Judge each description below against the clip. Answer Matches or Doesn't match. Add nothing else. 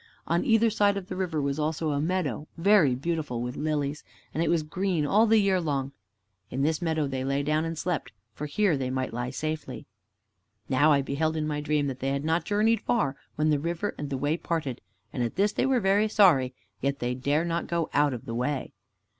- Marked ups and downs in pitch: Doesn't match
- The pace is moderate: Doesn't match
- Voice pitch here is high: Doesn't match